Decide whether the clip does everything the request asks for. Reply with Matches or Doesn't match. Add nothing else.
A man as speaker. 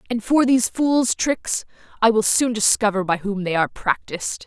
Doesn't match